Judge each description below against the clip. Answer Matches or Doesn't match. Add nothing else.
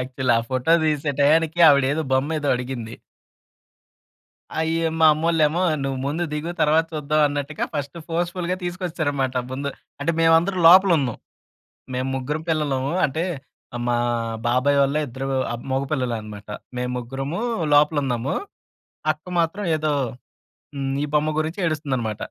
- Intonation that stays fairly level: Doesn't match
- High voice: Doesn't match